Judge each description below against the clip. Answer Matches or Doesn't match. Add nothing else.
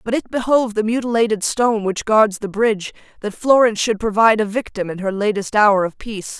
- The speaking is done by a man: Doesn't match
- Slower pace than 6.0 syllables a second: Doesn't match